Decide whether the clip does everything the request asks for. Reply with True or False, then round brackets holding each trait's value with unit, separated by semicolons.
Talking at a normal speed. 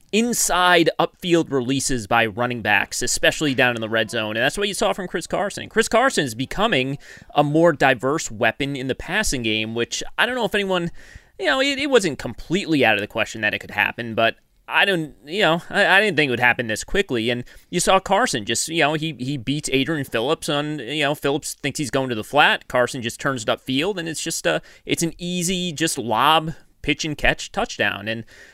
False (225 wpm)